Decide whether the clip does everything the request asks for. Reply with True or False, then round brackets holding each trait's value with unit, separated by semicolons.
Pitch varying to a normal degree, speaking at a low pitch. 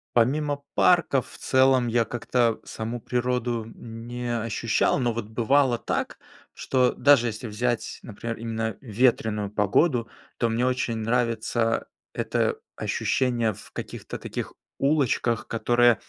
False (1.9 semitones; 120 Hz)